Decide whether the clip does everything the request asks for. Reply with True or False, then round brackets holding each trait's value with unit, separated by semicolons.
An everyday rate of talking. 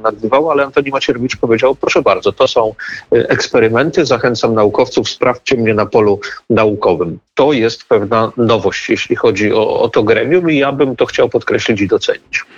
False (165 wpm)